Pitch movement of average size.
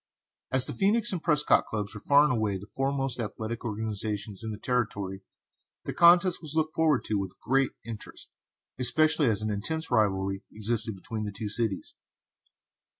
No: wide, 5.7 semitones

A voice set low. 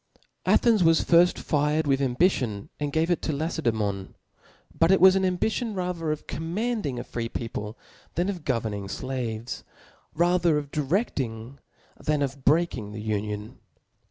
No: medium, 150 Hz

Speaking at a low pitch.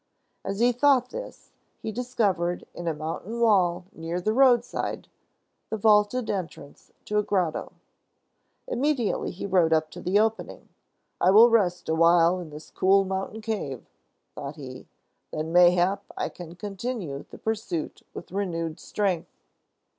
No: high, 190 Hz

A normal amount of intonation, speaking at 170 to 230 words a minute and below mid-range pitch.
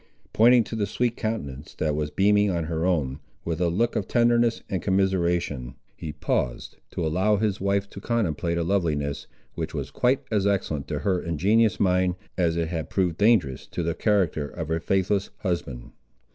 Yes: average, 4.2 semitones; average, 180 wpm; very low, 90 Hz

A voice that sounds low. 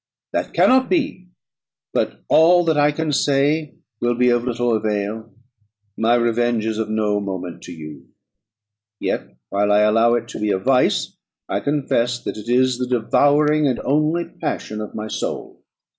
Yes: low, 120 Hz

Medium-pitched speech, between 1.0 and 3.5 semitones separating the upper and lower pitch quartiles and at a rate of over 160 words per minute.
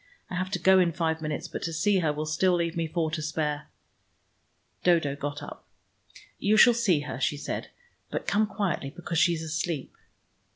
Yes: medium, 165 Hz; average, 3.0 semitones; average, 195 wpm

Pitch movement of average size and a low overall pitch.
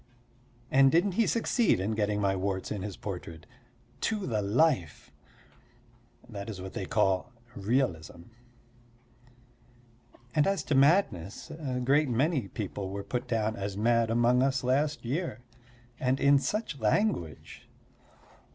No: wide, 6.1 semitones; low, 120 Hz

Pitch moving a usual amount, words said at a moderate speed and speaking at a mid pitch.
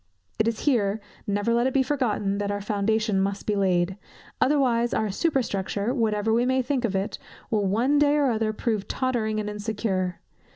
No: average, 3.4 semitones; average, 180 wpm; high, 220 Hz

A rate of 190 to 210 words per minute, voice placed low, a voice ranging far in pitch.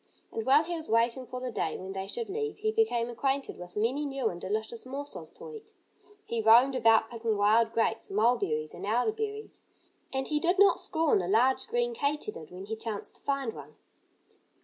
No: average, 195 wpm; high, 245 Hz; wide, 6.2 semitones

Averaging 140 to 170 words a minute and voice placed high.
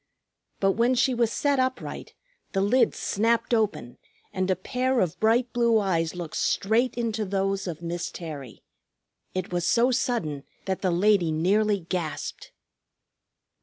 Yes: average, 145 wpm; high, 200 Hz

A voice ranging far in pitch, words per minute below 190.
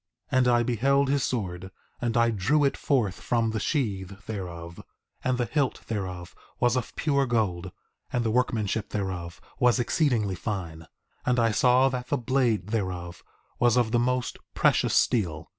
No: average, 4.8 semitones; average, 165 wpm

